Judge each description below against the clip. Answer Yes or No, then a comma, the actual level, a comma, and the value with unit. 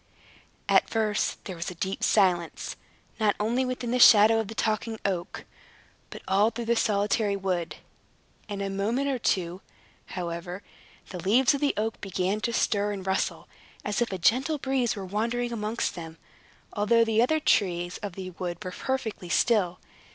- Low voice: No, high, 210 Hz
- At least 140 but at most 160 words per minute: No, average, 170 wpm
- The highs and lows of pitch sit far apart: No, average, 3.8 semitones